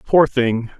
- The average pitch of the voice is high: No, low, 130 Hz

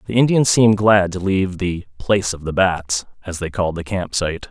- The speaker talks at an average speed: No, fast, 225 wpm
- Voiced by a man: Yes, male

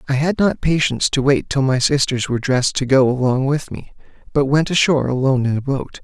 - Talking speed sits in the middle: No, fast, 230 wpm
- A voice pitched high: No, low, 135 Hz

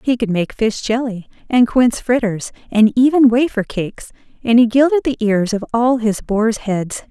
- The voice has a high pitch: Yes, high, 230 Hz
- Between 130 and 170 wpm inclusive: No, average, 185 wpm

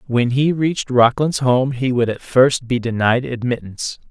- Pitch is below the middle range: Yes, low, 125 Hz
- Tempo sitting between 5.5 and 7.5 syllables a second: No, 4.7 syllables/s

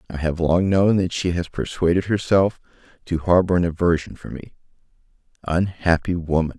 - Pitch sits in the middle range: No, very low, 85 Hz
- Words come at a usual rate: Yes, average, 155 wpm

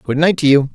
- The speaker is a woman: No, male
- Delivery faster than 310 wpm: Yes, fast, 320 wpm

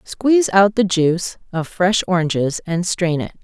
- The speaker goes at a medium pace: Yes, average, 175 wpm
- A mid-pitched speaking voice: Yes, medium, 180 Hz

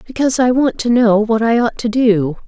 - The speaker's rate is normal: No, fast, 240 wpm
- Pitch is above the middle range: Yes, high, 230 Hz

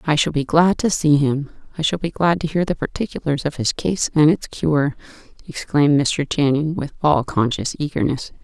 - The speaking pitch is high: No, medium, 150 Hz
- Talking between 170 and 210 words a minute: Yes, average, 200 wpm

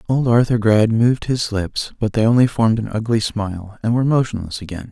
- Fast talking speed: Yes, fast, 210 wpm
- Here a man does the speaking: Yes, male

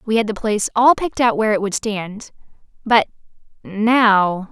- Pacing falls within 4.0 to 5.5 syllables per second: Yes, 5.0 syllables/s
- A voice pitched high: Yes, high, 215 Hz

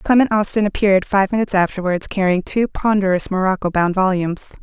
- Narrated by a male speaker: No, female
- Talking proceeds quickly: No, average, 155 wpm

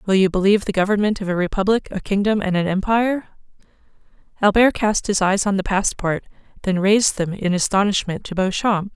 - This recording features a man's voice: No, female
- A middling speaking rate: Yes, average, 180 wpm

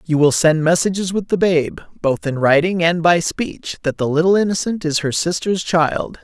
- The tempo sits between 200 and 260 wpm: No, average, 185 wpm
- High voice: No, medium, 170 Hz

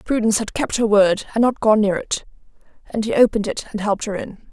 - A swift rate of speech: Yes, fast, 240 wpm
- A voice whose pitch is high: Yes, high, 220 Hz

